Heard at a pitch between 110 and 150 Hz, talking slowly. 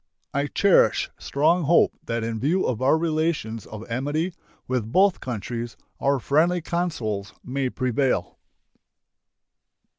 Yes: low, 135 Hz; slow, 120 wpm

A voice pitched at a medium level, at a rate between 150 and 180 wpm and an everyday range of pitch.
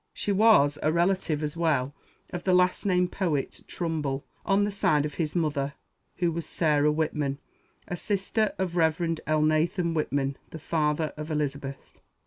Yes: medium, 160 Hz; average, 155 wpm; average, 3.1 semitones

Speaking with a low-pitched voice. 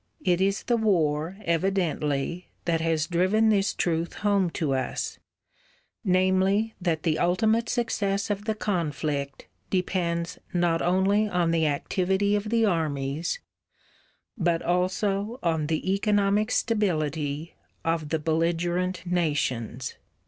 No: medium, 175 Hz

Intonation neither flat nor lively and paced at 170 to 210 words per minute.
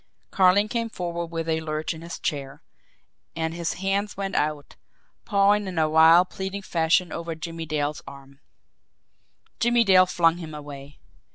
No: average, 3.7 semitones; average, 155 wpm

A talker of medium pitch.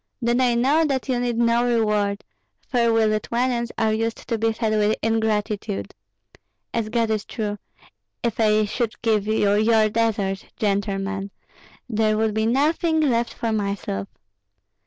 No: high, 220 Hz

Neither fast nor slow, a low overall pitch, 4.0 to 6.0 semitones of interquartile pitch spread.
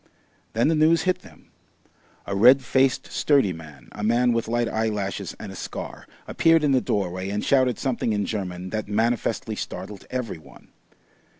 Yes: average, 170 wpm; low, 115 Hz; average, 4.6 semitones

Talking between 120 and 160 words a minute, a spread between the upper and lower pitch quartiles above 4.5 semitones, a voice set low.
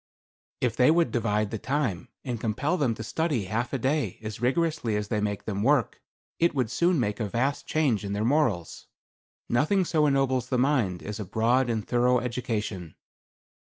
No: average, 185 wpm; average, 4.9 semitones; low, 120 Hz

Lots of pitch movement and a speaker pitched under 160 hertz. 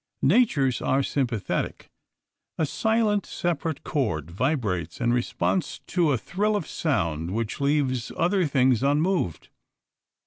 Yes: wide, 6.5 semitones; medium, 140 Hz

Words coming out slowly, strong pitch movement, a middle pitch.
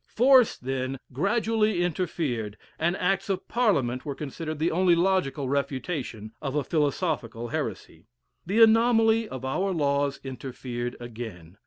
Yes: slow, 130 wpm; wide, 7.0 semitones; medium, 145 Hz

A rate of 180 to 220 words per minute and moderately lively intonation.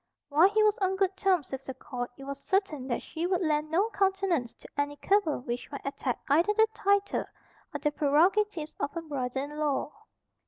No: average, 200 wpm; wide, 5.7 semitones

